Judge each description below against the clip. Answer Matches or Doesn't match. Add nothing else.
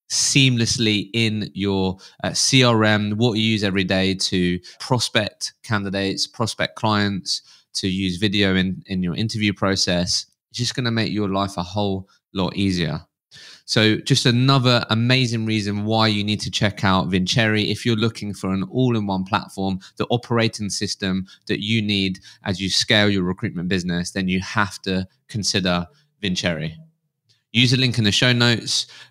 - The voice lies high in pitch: Doesn't match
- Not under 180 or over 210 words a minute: Doesn't match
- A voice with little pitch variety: Doesn't match